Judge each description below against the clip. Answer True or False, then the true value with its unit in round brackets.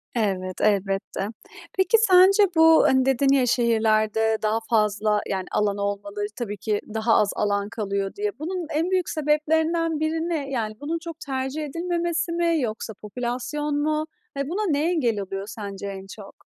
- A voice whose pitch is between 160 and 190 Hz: False (245 Hz)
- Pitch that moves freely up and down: True (7.3 semitones)